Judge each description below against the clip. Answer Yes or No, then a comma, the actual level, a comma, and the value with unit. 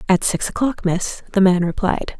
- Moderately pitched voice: No, high, 195 Hz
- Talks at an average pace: Yes, average, 190 wpm